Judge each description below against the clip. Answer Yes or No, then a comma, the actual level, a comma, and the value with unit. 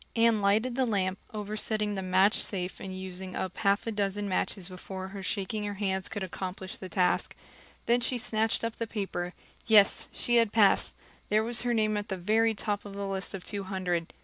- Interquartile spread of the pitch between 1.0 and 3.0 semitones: Yes, narrow, 2.5 semitones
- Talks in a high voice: Yes, high, 200 Hz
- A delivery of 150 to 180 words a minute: No, average, 200 wpm